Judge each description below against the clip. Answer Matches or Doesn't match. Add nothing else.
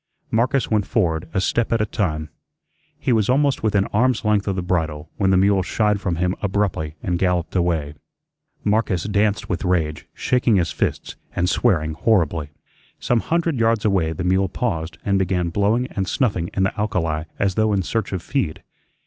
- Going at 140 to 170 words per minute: Doesn't match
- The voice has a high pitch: Doesn't match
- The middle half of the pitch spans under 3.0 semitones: Doesn't match